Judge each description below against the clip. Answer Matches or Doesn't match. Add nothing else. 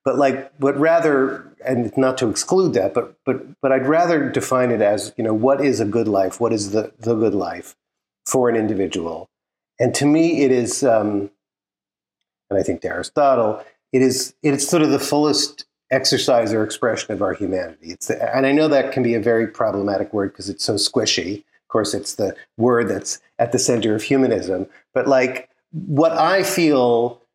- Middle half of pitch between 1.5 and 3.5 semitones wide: Doesn't match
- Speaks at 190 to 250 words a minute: Matches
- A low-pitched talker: Matches